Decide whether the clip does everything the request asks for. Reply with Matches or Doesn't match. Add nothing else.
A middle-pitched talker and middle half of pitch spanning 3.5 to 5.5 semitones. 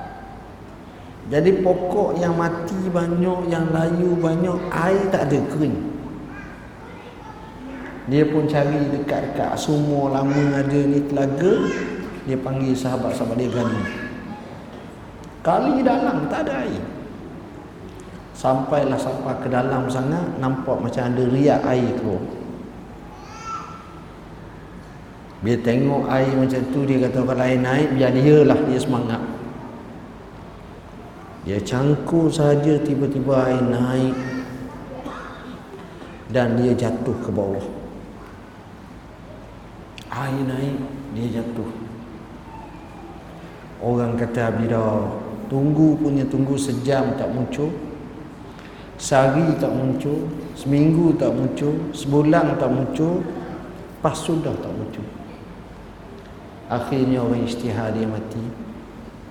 Doesn't match